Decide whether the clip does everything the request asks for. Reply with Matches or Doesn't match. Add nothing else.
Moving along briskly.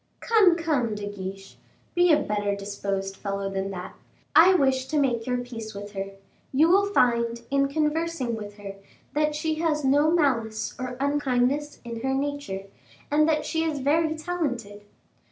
Doesn't match